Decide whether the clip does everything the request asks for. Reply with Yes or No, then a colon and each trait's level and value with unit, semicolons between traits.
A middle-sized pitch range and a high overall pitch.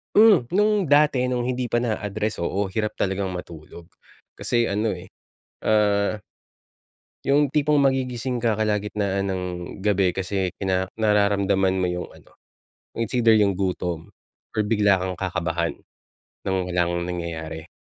No: average, 4.2 semitones; low, 100 Hz